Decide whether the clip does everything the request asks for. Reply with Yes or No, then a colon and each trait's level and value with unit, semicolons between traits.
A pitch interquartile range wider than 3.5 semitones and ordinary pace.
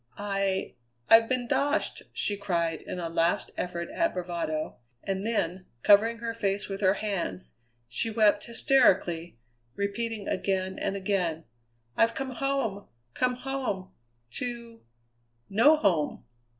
No: average, 4.2 semitones; slow, 125 wpm